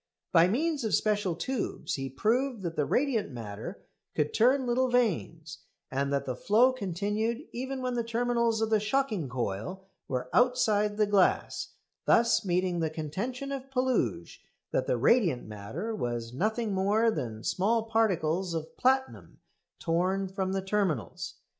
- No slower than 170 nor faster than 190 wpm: No, average, 150 wpm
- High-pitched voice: Yes, high, 205 Hz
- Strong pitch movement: Yes, wide, 6.6 semitones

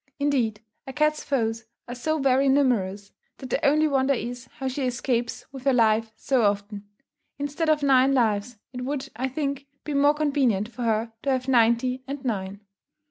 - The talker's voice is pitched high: Yes, very high, 255 Hz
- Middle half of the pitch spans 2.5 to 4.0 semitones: Yes, average, 3.5 semitones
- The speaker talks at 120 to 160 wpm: No, average, 180 wpm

